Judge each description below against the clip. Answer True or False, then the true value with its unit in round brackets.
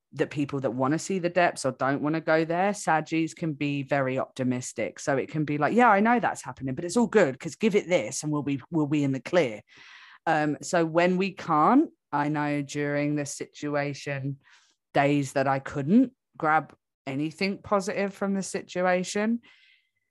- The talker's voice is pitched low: False (155 Hz)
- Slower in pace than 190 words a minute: False (195 wpm)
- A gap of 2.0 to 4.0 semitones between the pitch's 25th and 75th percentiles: False (5.2 semitones)